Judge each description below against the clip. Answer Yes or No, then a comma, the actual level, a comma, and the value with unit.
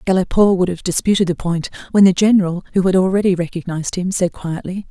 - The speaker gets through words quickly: No, average, 195 wpm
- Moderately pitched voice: Yes, medium, 180 Hz